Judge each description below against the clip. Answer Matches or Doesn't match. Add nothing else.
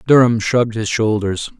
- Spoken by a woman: Doesn't match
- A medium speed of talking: Matches